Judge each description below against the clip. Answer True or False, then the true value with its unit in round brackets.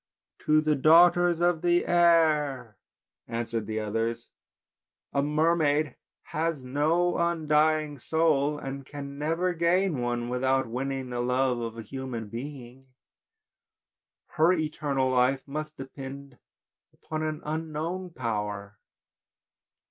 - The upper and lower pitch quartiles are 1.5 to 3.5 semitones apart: False (4.1 semitones)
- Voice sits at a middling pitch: True (145 Hz)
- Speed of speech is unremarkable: False (110 wpm)